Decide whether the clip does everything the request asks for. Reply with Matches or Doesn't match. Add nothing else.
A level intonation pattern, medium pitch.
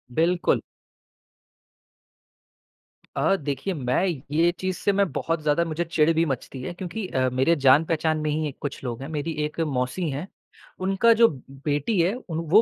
Doesn't match